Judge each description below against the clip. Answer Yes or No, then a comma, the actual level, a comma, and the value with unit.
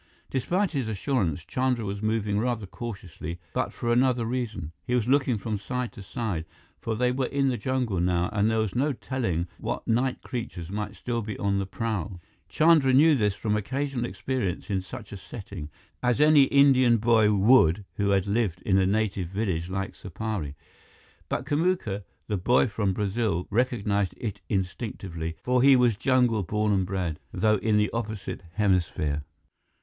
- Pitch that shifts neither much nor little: Yes, average, 4.5 semitones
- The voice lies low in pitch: Yes, low, 110 Hz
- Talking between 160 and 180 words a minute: Yes, average, 170 wpm